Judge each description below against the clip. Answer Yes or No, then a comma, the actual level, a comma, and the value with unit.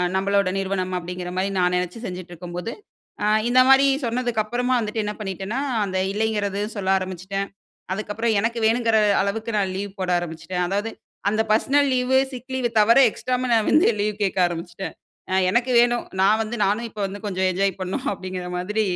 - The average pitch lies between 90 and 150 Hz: No, high, 205 Hz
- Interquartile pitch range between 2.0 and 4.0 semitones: Yes, average, 3.7 semitones